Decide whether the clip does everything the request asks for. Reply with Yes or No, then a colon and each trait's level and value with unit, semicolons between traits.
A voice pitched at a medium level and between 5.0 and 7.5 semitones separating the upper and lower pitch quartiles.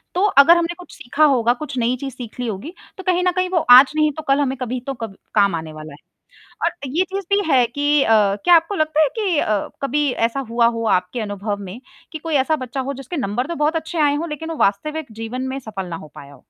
No: very high, 275 Hz; wide, 5.5 semitones